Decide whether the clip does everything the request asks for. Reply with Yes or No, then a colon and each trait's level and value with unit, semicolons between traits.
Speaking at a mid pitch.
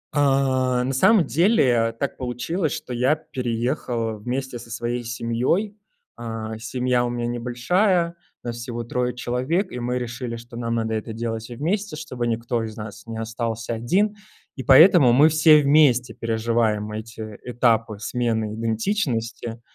No: low, 120 Hz